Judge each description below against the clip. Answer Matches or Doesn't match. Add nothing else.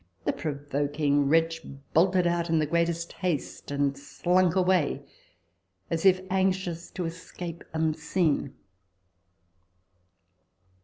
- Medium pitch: Matches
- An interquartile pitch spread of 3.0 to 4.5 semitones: Matches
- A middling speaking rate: Doesn't match